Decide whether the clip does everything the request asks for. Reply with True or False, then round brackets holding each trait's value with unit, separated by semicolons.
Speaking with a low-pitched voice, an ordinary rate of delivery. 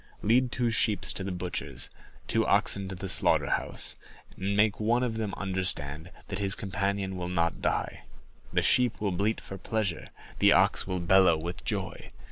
True (95 Hz; 170 wpm)